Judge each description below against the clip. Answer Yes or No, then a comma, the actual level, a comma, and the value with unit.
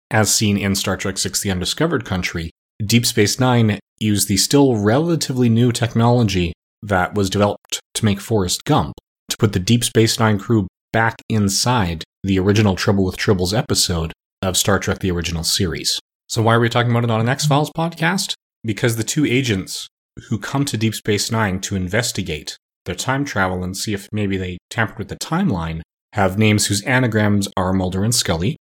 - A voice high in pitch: No, low, 105 Hz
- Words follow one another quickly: No, average, 190 wpm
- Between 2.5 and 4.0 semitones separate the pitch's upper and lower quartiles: Yes, average, 3.6 semitones